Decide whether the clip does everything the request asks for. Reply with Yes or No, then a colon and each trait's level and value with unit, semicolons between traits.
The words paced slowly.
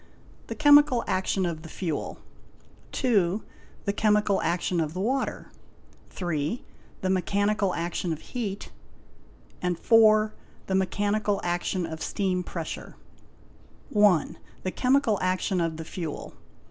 Yes: slow, 115 wpm